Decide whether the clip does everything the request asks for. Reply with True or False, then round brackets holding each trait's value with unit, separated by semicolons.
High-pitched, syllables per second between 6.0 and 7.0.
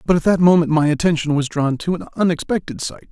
False (165 Hz; 6.2 syllables/s)